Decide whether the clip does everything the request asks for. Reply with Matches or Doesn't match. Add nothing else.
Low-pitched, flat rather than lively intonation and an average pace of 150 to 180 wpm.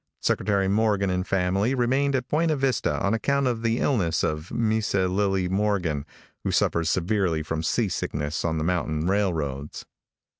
Doesn't match